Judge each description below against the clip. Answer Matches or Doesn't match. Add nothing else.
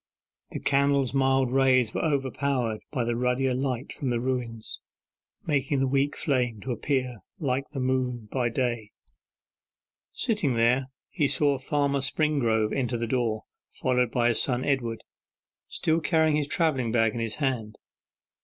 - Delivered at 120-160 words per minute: Matches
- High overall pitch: Doesn't match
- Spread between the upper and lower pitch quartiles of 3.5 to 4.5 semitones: Doesn't match